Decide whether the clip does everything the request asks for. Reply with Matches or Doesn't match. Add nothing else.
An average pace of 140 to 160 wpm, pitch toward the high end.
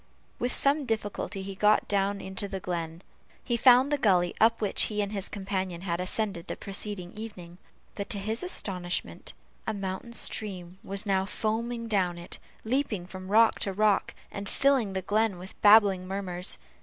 Doesn't match